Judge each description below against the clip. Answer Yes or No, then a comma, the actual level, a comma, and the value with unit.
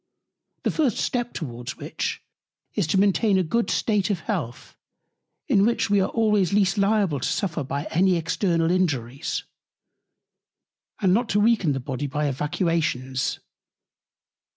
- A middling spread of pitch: No, wide, 5.9 semitones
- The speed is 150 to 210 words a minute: No, average, 140 wpm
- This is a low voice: No, medium, 185 Hz